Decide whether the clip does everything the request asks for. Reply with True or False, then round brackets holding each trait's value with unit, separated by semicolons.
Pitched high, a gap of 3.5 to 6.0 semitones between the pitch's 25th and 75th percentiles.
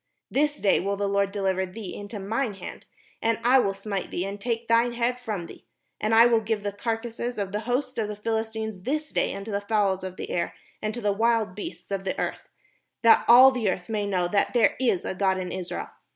False (210 Hz; 2.8 semitones)